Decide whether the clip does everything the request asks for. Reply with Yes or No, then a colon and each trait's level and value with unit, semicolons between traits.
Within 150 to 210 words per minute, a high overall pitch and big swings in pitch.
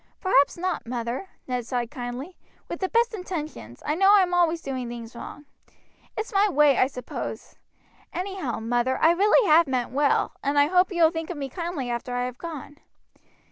Yes: average, 190 wpm; very high, 295 Hz; wide, 6.3 semitones